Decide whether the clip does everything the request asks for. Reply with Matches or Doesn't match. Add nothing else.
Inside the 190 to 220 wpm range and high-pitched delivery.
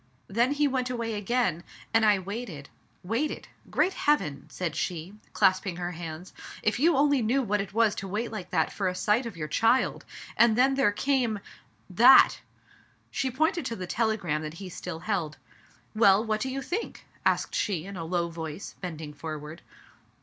Matches